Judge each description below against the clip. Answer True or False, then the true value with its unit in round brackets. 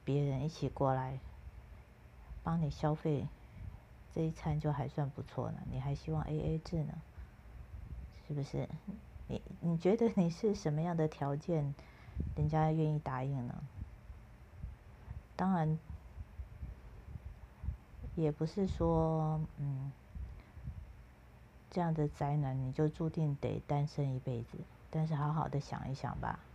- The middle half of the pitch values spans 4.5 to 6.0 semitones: False (3.2 semitones)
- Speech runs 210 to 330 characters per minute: False (180 characters per minute)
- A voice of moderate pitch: True (150 Hz)